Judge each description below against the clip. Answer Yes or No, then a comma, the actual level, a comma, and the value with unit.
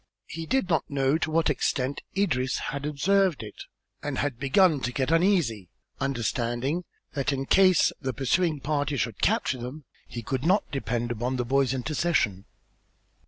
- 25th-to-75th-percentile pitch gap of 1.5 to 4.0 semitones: No, average, 4.5 semitones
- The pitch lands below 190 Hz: Yes, medium, 140 Hz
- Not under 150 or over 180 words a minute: Yes, average, 160 wpm